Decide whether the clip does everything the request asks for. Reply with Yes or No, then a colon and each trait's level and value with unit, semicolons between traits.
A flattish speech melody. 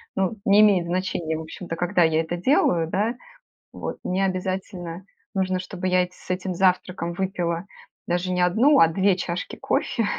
Yes: narrow, 1.8 semitones